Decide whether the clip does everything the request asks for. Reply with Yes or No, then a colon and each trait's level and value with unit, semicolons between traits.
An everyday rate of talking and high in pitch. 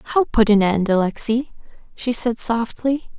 Yes: average, 150 wpm; high, 230 Hz